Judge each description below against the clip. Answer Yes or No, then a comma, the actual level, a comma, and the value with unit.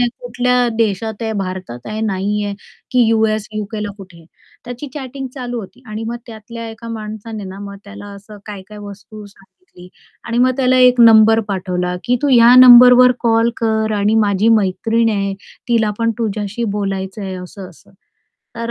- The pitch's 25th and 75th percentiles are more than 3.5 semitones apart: No, average, 2.7 semitones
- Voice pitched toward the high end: Yes, high, 220 Hz